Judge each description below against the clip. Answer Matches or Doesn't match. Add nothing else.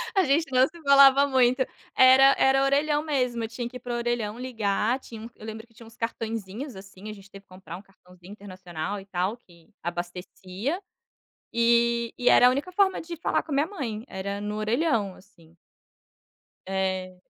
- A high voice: Matches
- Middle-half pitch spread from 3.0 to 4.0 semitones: Doesn't match